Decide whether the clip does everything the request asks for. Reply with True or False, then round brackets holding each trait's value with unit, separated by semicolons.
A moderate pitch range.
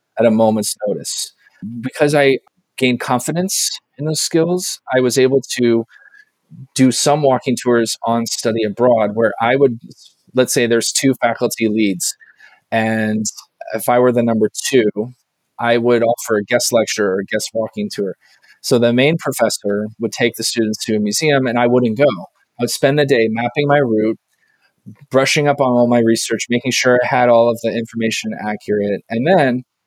True (3.1 semitones)